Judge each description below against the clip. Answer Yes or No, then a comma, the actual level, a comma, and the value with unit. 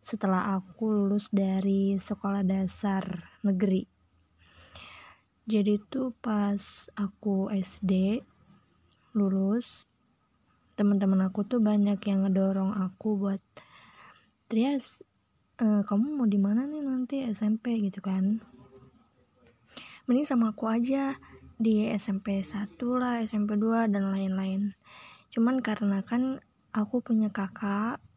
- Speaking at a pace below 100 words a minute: No, average, 105 wpm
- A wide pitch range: No, narrow, 2.6 semitones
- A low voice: No, high, 205 Hz